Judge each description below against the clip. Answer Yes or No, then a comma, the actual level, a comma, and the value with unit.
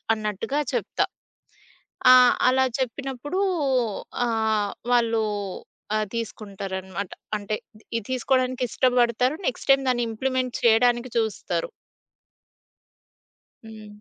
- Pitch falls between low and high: No, high, 235 Hz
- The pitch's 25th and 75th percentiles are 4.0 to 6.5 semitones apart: No, average, 2.9 semitones